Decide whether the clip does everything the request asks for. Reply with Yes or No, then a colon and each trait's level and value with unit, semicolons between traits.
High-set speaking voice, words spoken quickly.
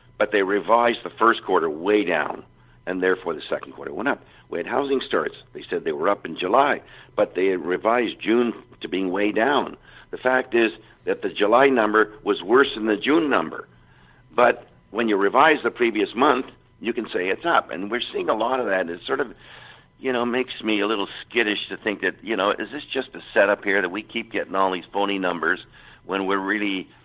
No: low, 120 Hz; fast, 215 wpm